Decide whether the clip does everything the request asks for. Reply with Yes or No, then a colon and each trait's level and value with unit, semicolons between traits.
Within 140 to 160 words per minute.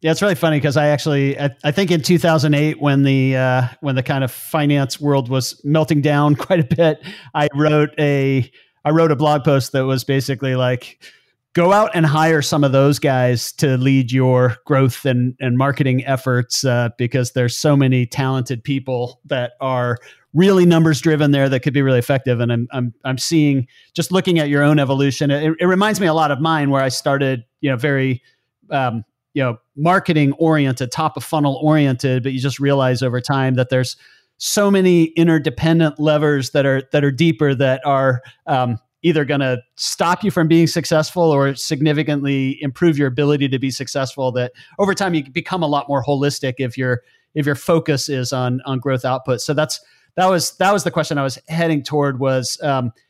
No: average, 195 wpm